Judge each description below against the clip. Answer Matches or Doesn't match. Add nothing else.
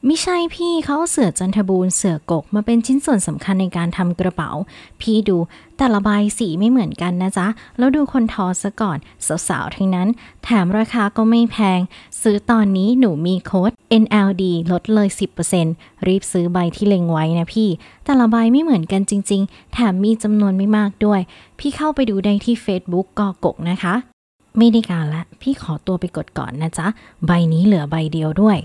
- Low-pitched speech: Doesn't match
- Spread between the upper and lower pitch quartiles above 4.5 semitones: Doesn't match